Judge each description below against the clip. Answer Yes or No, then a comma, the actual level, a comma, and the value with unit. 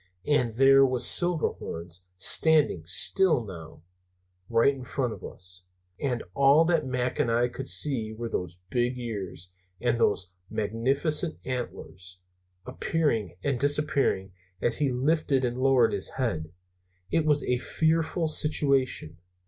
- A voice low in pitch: Yes, low, 125 Hz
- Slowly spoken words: Yes, slow, 130 wpm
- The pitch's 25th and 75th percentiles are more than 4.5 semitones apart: Yes, average, 4.9 semitones